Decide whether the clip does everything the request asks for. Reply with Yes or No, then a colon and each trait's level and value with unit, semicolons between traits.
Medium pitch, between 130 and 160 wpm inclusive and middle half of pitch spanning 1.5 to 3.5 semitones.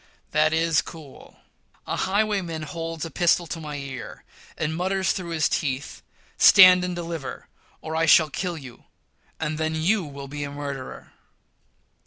Yes: medium, 160 Hz; average, 150 wpm; average, 2.9 semitones